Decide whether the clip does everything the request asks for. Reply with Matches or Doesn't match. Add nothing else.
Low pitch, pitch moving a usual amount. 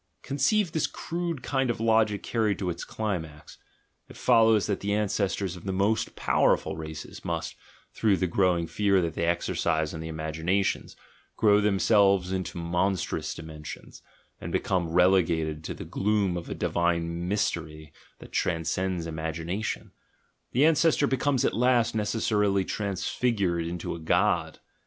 Matches